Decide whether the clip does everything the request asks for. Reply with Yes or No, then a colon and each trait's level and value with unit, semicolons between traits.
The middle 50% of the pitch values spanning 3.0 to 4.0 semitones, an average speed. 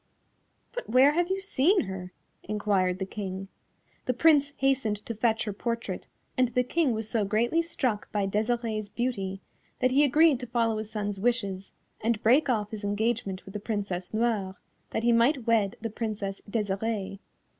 Yes: average, 3.6 semitones; average, 170 wpm